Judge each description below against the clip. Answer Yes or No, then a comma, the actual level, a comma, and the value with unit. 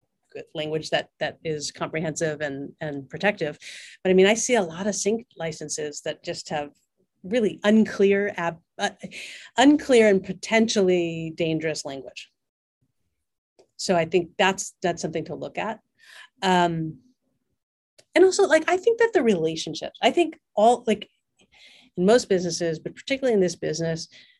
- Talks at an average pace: Yes, average, 145 wpm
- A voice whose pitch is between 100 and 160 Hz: No, medium, 180 Hz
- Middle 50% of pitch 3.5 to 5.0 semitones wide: No, wide, 5.6 semitones